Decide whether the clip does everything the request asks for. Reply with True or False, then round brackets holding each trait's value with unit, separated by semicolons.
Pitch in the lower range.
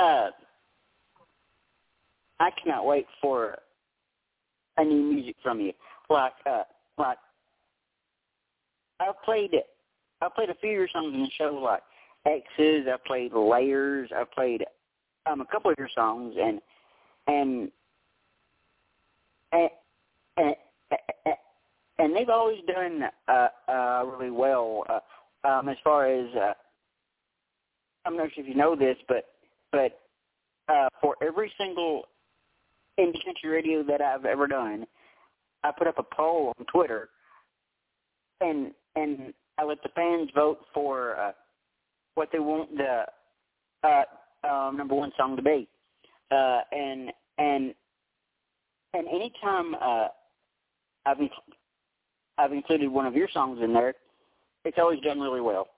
False (150 Hz)